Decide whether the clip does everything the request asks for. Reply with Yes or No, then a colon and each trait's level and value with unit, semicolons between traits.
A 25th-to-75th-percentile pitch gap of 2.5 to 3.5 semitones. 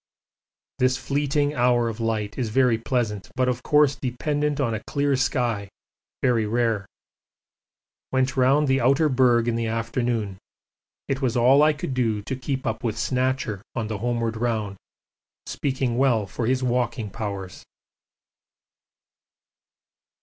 Yes: average, 2.8 semitones